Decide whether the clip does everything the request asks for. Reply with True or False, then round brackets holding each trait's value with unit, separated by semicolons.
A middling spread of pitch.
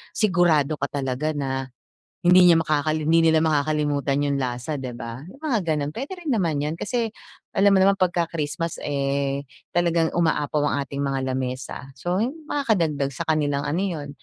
True (3.8 semitones)